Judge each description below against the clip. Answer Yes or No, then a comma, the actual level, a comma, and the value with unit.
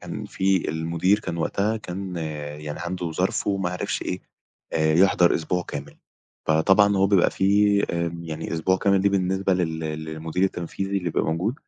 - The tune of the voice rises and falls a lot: No, average, 3.2 semitones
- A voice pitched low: Yes, very low, 90 Hz